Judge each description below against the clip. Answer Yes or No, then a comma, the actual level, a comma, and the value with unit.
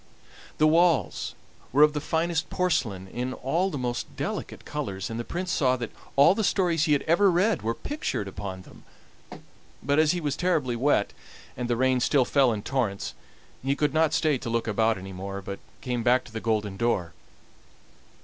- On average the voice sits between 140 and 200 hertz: No, low, 130 Hz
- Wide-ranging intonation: Yes, wide, 5.9 semitones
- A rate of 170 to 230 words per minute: Yes, average, 190 wpm